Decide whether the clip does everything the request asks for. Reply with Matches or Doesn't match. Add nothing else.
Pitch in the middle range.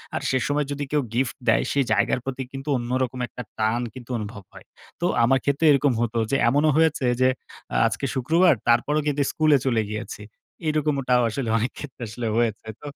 Doesn't match